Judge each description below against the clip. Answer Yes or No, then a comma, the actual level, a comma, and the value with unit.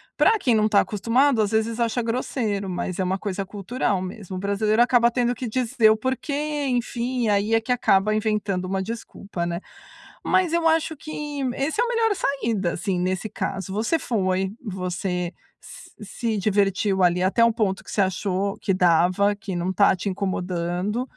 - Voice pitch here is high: Yes, high, 210 Hz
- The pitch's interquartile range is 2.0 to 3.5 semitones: No, average, 4.1 semitones